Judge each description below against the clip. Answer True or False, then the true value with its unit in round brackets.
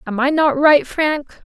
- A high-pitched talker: True (280 Hz)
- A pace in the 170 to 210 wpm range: True (200 wpm)